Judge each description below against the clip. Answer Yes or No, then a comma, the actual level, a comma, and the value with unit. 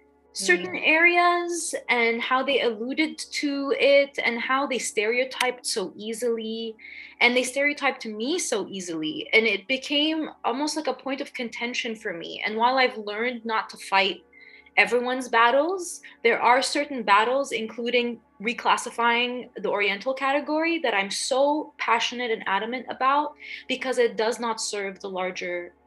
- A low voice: No, high, 245 Hz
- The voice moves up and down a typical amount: Yes, average, 4.0 semitones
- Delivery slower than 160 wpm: Yes, average, 145 wpm